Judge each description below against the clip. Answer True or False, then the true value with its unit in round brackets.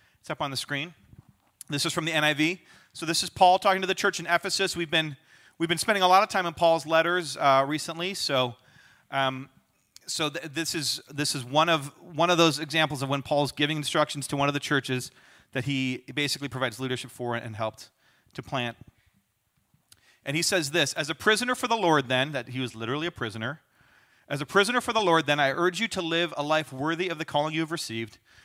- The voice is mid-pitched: True (150 Hz)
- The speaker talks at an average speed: False (220 wpm)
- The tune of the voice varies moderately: True (4.1 semitones)